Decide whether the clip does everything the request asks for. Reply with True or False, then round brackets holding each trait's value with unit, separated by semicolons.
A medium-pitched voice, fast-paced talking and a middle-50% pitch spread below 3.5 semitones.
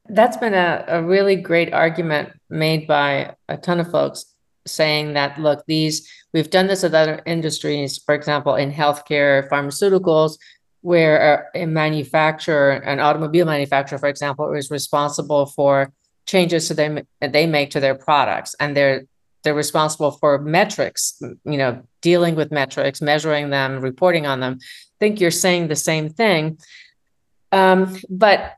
False (155 Hz; 150 wpm; 2.8 semitones)